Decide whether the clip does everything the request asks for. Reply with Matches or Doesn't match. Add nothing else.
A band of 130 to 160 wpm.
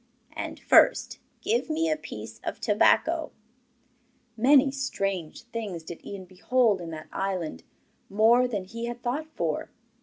Matches